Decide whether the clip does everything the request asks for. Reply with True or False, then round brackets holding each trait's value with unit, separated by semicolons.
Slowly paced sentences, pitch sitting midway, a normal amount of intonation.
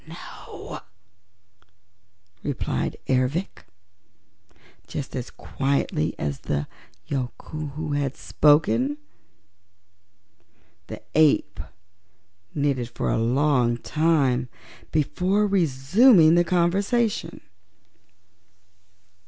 True (70 wpm; 145 Hz; 4.7 semitones)